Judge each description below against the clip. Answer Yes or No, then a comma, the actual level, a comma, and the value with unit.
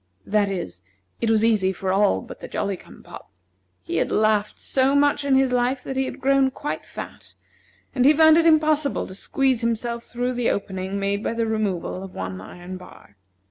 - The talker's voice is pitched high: Yes, high, 225 Hz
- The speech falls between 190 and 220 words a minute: Yes, average, 200 wpm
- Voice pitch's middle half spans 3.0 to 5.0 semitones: No, wide, 5.5 semitones